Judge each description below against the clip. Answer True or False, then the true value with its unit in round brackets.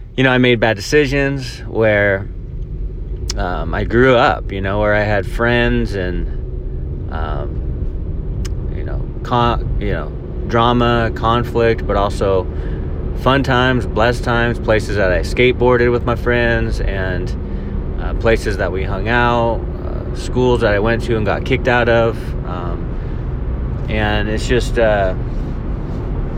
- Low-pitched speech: True (110 Hz)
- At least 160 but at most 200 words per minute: False (140 wpm)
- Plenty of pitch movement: False (4.3 semitones)